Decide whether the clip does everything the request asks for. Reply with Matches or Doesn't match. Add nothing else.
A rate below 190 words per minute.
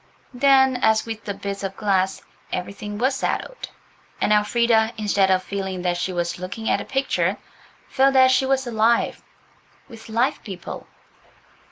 Matches